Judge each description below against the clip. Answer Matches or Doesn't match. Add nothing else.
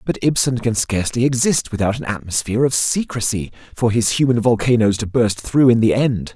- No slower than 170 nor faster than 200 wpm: Matches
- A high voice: Doesn't match